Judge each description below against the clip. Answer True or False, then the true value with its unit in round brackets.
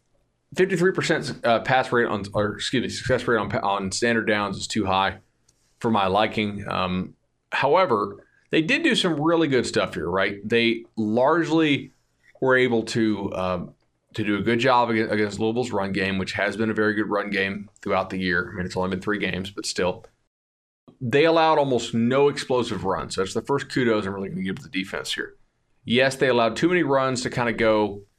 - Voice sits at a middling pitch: False (110 Hz)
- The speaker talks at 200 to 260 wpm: True (205 wpm)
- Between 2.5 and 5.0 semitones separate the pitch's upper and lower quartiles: True (4.5 semitones)